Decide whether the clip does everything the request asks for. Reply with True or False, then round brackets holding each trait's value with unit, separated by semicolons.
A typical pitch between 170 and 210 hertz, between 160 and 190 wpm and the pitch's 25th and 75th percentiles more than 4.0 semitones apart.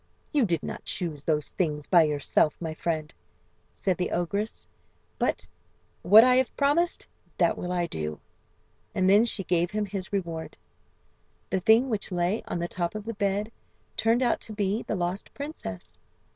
True (185 Hz; 170 wpm; 4.4 semitones)